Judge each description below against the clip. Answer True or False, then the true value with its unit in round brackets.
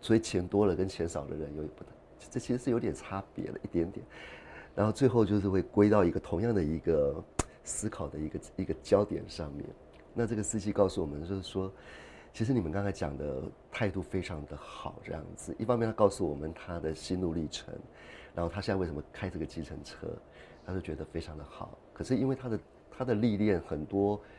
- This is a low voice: True (95 Hz)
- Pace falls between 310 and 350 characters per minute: True (315 characters per minute)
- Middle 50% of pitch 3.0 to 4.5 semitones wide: False (5.2 semitones)